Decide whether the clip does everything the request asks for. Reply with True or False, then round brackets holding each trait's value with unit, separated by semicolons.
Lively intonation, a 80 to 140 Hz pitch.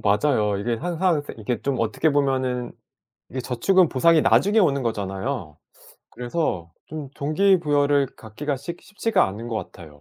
True (5.8 semitones; 135 Hz)